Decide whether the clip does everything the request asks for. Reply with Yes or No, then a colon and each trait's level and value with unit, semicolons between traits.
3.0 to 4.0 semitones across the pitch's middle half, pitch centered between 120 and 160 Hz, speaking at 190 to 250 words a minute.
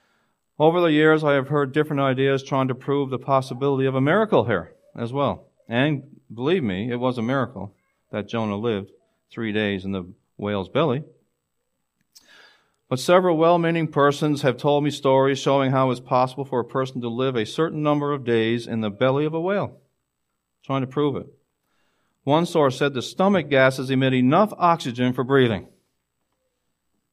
No: average, 3.6 semitones; low, 135 Hz; average, 175 wpm